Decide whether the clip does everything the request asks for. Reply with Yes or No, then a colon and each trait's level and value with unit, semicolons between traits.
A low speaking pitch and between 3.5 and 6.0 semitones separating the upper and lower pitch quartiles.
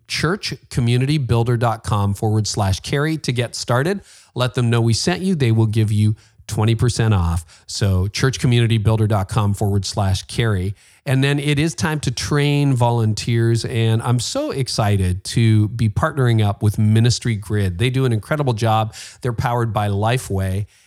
No: low, 115 Hz; average, 3.1 semitones